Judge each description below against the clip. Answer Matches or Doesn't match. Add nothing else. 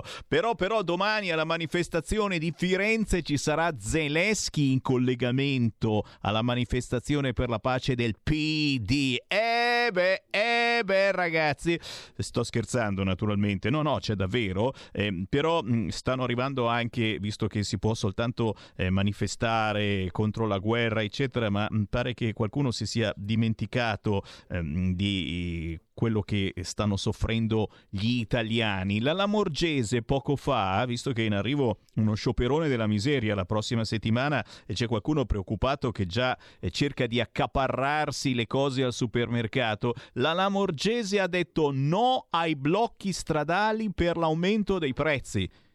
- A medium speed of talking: Matches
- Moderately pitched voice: Doesn't match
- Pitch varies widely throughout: Matches